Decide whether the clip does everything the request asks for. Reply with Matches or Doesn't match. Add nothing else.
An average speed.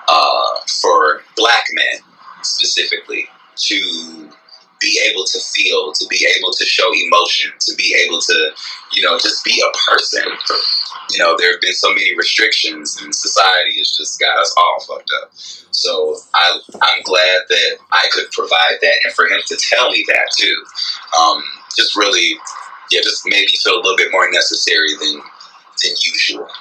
Matches